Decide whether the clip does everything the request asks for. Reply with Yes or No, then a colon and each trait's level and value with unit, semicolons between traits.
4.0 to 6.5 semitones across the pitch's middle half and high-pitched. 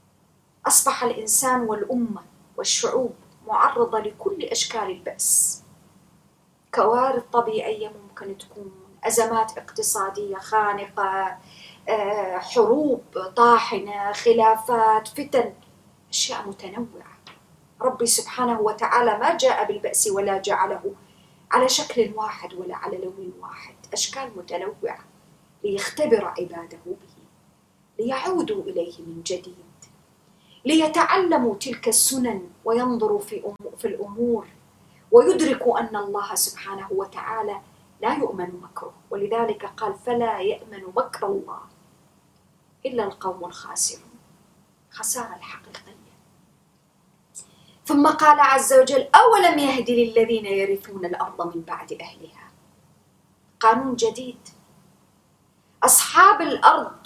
Yes: average, 5.3 semitones; high, 225 Hz